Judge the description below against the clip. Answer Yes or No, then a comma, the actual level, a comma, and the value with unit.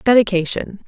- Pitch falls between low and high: No, high, 205 Hz